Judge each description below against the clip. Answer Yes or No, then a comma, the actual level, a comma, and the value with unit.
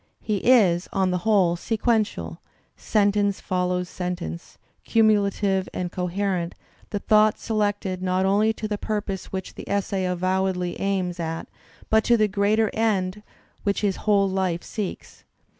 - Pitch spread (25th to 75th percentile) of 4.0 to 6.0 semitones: No, narrow, 2.5 semitones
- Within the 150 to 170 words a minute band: No, average, 140 wpm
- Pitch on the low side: No, high, 195 Hz